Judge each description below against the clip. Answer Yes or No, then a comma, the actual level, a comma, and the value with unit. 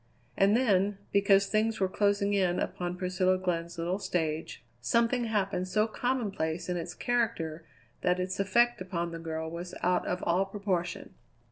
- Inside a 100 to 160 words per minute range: Yes, average, 155 wpm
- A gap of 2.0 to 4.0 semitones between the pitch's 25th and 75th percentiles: Yes, average, 2.8 semitones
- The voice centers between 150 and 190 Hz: Yes, medium, 185 Hz